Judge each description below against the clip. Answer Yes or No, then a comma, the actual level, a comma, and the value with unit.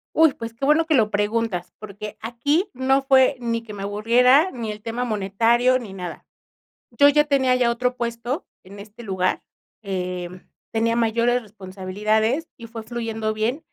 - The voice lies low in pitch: No, high, 230 Hz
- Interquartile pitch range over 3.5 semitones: No, average, 3.2 semitones